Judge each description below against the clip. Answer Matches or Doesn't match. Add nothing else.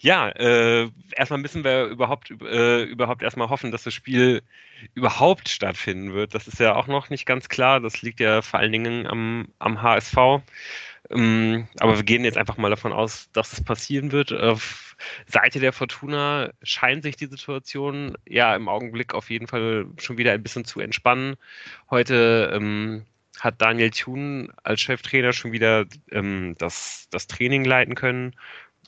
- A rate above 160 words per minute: Matches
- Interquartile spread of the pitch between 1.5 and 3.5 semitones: Matches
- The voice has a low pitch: Matches